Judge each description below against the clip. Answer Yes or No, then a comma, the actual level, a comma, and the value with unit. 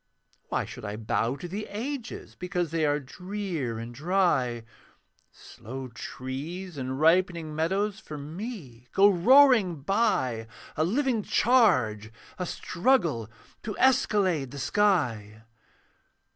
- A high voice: No, medium, 170 Hz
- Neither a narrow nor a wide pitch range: No, wide, 7.8 semitones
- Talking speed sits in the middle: No, slow, 115 wpm